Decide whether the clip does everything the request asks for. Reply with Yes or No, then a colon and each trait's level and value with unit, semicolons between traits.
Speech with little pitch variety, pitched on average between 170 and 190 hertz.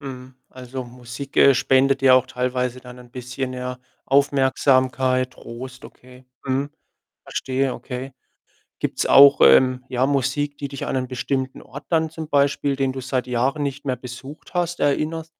No: narrow, 1.6 semitones; low, 130 Hz